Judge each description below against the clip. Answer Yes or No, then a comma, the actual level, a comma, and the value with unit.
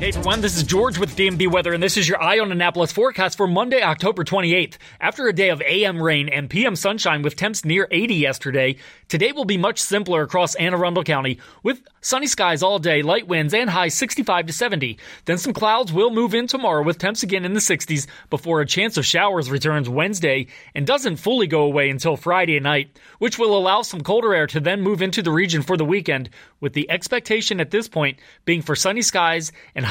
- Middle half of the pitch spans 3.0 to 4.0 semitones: No, average, 4.7 semitones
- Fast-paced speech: Yes, fast, 220 wpm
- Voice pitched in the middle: Yes, medium, 180 Hz